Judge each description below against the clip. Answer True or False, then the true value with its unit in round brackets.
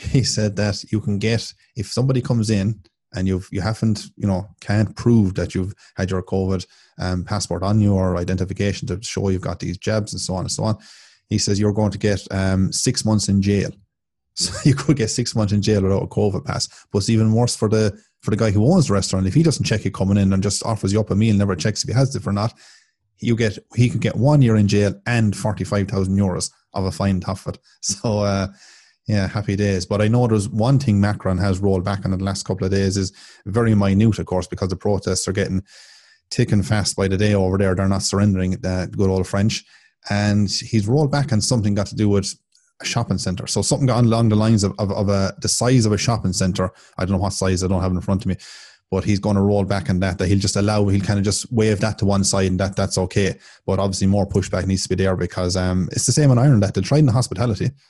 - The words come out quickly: True (260 wpm)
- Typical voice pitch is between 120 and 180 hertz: False (100 Hz)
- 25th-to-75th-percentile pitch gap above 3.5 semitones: False (2.5 semitones)